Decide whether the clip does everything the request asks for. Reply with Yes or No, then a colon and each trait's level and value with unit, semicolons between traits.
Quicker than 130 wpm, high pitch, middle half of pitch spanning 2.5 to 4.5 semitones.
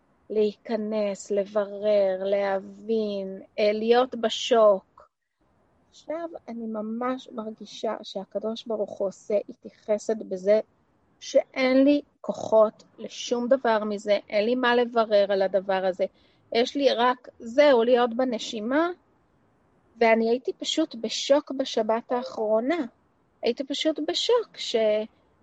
No: average, 105 wpm; high, 225 Hz; average, 3.7 semitones